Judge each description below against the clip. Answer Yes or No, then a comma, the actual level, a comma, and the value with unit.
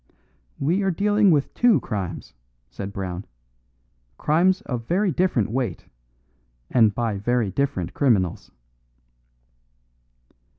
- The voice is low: Yes, low, 125 Hz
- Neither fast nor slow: No, slow, 100 wpm